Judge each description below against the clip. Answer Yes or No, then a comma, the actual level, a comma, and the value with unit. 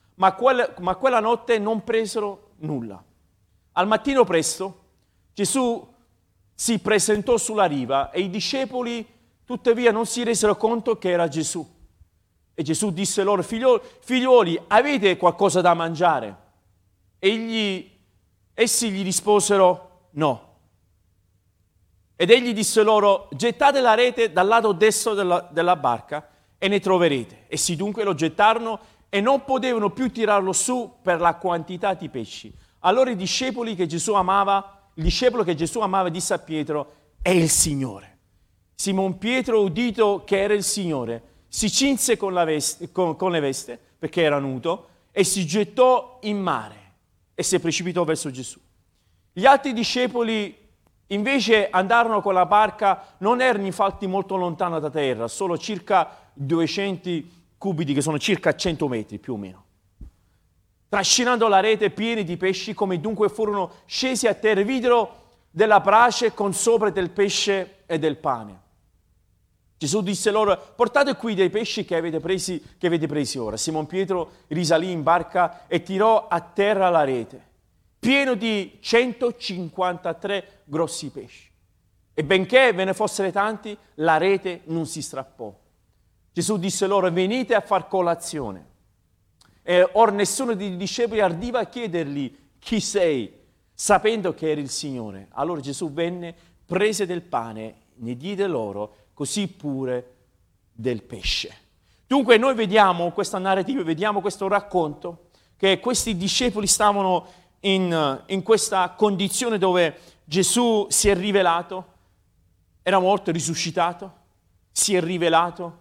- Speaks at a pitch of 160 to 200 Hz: Yes, medium, 185 Hz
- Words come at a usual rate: Yes, average, 140 wpm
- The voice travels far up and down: Yes, wide, 6.2 semitones